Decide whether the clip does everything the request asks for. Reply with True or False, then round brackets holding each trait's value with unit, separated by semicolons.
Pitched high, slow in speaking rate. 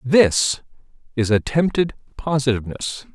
False (135 Hz; 75 wpm)